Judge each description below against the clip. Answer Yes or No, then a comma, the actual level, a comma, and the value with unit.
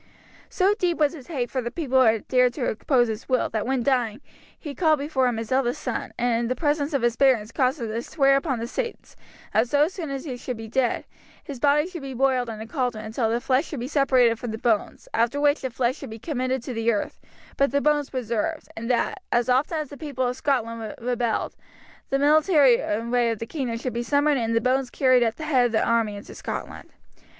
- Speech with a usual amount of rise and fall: Yes, average, 3.4 semitones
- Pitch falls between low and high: No, very high, 255 Hz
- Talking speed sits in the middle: No, fast, 240 wpm